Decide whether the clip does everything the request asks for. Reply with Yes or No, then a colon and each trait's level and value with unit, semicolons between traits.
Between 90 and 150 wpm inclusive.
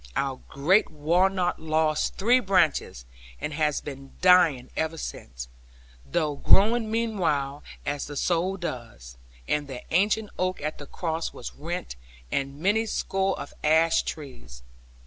Yes: slow, 135 wpm